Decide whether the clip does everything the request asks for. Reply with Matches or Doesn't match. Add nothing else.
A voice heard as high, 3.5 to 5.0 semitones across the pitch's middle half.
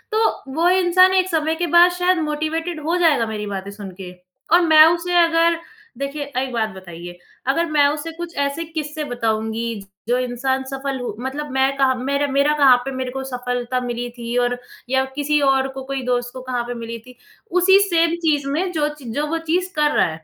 Matches